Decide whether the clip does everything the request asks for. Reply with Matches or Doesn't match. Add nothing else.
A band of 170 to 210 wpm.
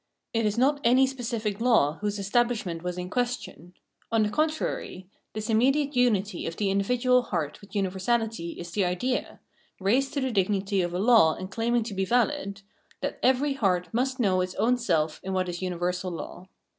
Matches